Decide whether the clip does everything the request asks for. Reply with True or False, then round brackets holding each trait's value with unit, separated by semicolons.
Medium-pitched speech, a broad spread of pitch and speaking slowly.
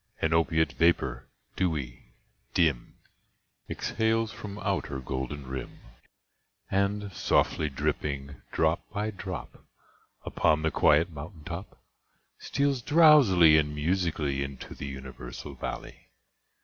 False (80 Hz; 5.8 semitones; 110 wpm)